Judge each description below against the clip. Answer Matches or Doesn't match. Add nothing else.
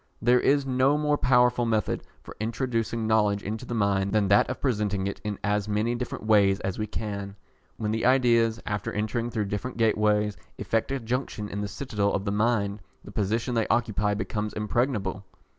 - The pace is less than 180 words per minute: Doesn't match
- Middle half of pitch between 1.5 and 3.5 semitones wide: Matches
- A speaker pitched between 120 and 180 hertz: Doesn't match